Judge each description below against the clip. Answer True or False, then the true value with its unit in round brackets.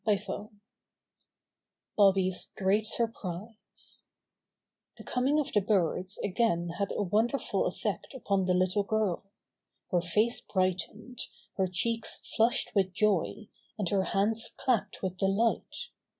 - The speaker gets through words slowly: True (125 wpm)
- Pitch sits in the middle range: False (200 Hz)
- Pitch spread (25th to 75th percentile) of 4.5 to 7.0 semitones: False (3.0 semitones)